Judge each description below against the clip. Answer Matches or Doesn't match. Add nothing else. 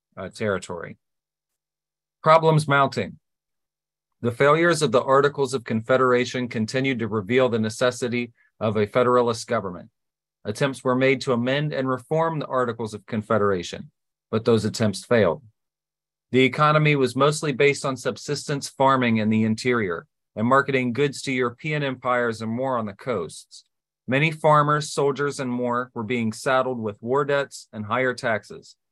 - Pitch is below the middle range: Matches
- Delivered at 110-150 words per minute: Matches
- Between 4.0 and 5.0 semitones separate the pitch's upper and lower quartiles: Doesn't match